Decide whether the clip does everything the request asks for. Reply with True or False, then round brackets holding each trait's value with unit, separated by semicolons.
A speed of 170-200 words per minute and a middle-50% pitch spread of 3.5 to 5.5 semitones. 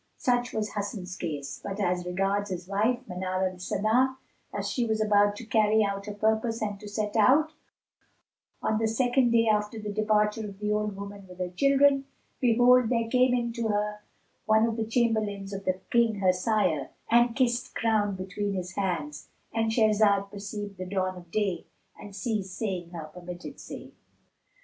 False (175 wpm; 2.8 semitones)